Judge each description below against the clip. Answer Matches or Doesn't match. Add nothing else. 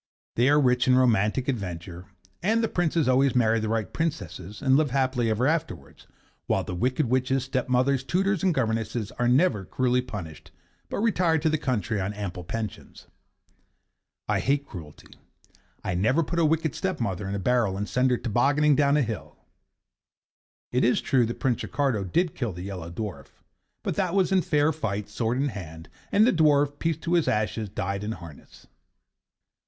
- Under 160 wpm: Doesn't match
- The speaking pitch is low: Matches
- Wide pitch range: Matches